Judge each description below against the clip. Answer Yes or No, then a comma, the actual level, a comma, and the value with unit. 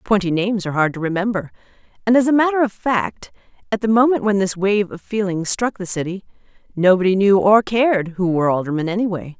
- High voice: Yes, high, 200 Hz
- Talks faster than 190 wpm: Yes, average, 200 wpm